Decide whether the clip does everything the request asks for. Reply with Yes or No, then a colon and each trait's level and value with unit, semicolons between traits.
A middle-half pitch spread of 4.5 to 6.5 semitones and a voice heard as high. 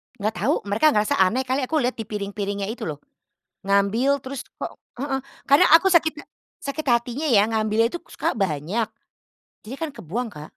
Yes: average, 5.0 semitones; high, 225 Hz